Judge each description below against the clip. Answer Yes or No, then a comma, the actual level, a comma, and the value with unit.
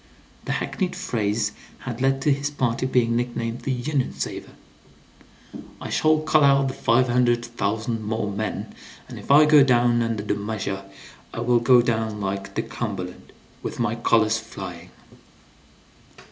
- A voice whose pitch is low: Yes, low, 120 Hz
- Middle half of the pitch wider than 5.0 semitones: No, average, 3.1 semitones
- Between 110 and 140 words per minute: No, average, 155 wpm